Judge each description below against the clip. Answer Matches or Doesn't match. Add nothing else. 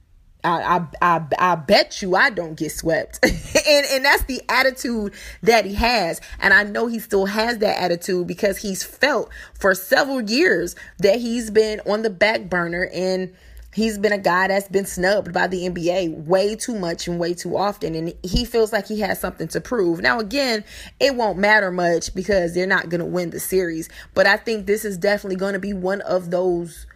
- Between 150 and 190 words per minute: Doesn't match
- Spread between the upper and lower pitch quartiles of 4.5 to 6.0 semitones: Doesn't match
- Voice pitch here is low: Doesn't match